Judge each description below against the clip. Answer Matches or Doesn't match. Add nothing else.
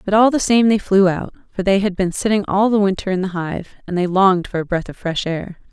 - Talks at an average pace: Doesn't match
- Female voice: Matches